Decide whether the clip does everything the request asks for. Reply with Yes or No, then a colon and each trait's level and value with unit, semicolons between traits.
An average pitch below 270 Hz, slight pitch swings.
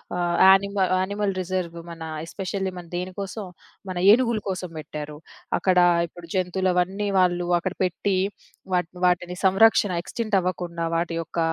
Yes: medium, 185 Hz; narrow, 1.8 semitones